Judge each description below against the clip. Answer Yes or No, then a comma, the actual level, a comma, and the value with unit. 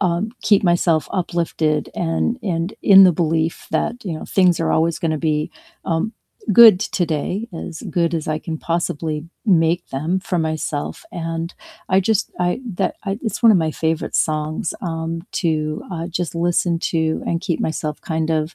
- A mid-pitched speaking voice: Yes, medium, 165 Hz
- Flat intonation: Yes, narrow, 2.2 semitones